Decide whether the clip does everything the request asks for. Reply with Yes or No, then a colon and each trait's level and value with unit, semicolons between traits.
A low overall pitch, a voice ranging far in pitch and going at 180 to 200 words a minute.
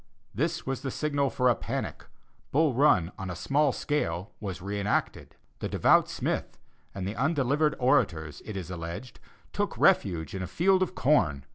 No: low, 115 Hz; wide, 7.9 semitones; average, 170 wpm